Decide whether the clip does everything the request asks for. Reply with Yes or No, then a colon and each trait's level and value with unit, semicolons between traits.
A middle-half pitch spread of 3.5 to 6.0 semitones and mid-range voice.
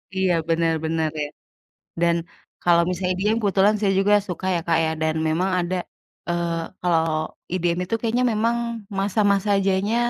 No: average, 3.0 semitones; medium, 180 Hz